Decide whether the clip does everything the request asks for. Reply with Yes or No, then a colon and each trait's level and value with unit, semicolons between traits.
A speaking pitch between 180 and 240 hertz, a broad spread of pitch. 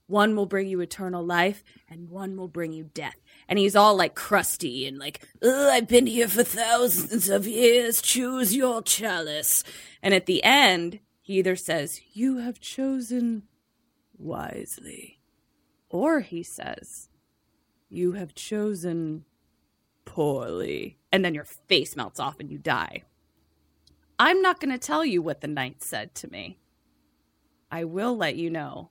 Yes: high, 190 Hz; wide, 7.0 semitones